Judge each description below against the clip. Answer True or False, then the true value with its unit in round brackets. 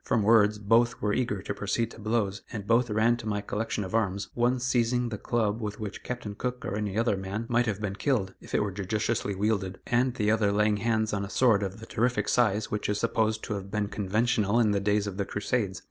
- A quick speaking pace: True (240 wpm)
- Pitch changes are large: False (2.4 semitones)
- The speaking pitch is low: True (105 Hz)